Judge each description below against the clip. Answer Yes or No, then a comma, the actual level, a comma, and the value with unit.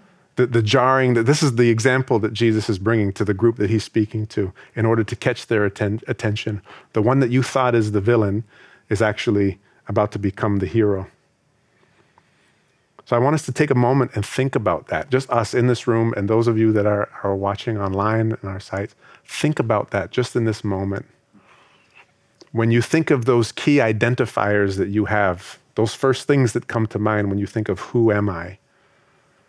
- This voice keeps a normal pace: No, fast, 210 wpm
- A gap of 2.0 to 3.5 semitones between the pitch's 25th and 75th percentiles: Yes, average, 2.9 semitones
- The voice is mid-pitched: No, low, 110 Hz